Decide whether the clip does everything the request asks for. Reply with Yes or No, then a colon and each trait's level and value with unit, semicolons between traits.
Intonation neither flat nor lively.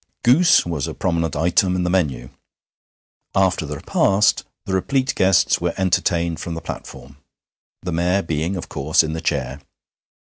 Yes: average, 3.3 semitones